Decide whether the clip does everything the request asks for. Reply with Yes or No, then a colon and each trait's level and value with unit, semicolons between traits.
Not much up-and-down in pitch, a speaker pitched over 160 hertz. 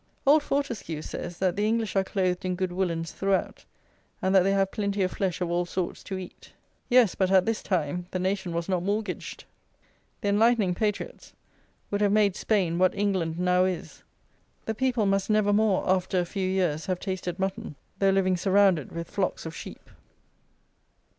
Yes: narrow, 2.2 semitones; high, 190 Hz